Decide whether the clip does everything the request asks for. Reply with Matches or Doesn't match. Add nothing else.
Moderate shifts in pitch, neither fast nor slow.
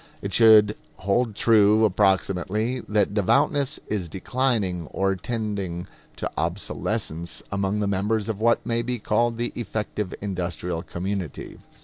Doesn't match